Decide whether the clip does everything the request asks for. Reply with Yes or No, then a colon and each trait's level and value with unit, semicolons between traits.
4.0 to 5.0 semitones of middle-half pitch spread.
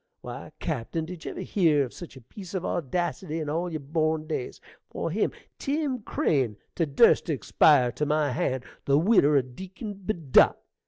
Yes: average, 4.5 semitones